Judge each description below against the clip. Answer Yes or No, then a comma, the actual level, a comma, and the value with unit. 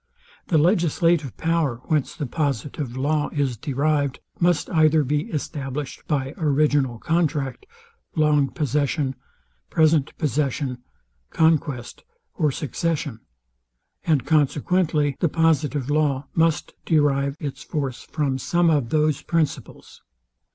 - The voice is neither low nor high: Yes, medium, 150 Hz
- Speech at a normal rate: No, slow, 110 wpm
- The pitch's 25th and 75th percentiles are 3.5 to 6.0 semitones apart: No, narrow, 2.5 semitones